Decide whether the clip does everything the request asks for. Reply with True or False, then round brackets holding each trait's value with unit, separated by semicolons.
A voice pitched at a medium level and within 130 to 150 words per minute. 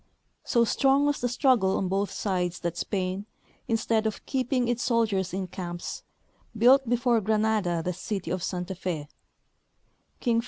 False (210 Hz; 145 wpm)